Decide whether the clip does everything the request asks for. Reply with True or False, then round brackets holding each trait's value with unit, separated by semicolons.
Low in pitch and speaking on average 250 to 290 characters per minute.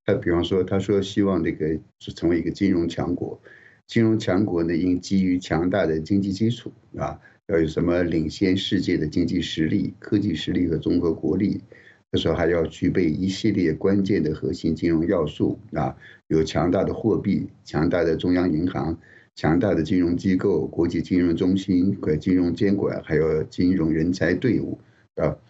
True (90 Hz; 275 characters per minute)